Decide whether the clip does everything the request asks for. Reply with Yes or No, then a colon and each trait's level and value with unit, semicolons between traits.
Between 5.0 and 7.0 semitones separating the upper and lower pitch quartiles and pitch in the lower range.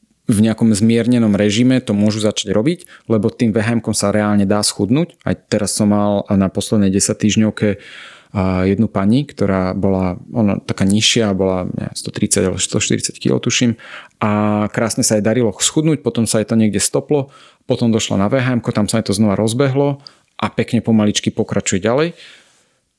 No: narrow, 2.5 semitones; low, 110 Hz